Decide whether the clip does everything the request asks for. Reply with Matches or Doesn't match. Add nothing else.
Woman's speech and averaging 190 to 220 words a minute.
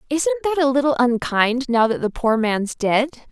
Matches